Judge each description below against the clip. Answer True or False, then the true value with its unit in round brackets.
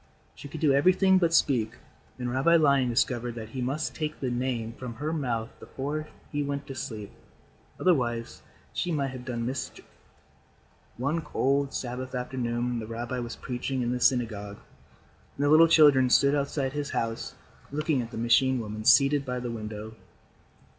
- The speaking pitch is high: False (130 Hz)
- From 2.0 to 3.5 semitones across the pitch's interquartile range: True (3.2 semitones)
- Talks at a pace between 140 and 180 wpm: True (165 wpm)